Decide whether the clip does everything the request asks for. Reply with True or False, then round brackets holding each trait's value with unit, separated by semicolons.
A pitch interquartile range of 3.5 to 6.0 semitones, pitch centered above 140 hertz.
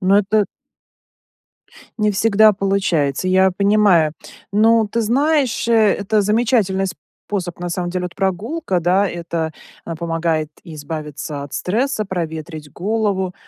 True (4.0 semitones; 190 Hz)